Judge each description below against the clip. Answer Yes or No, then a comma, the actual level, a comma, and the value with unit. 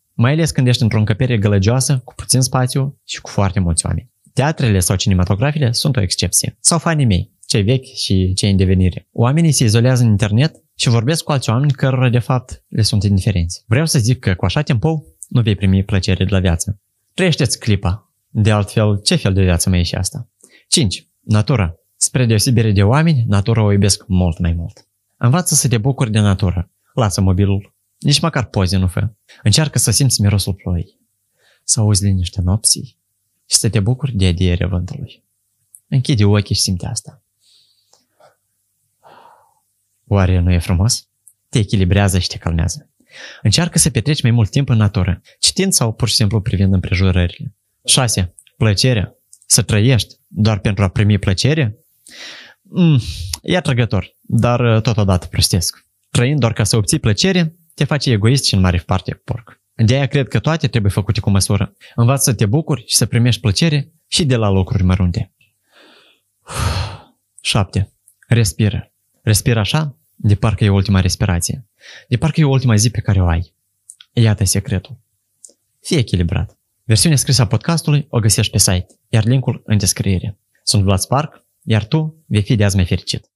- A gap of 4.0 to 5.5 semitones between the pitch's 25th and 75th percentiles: Yes, average, 4.5 semitones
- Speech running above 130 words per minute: Yes, fast, 170 wpm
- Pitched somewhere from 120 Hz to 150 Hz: No, low, 110 Hz